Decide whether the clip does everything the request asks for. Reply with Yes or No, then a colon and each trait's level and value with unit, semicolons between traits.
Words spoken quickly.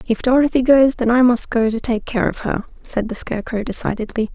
Yes: fast, 220 wpm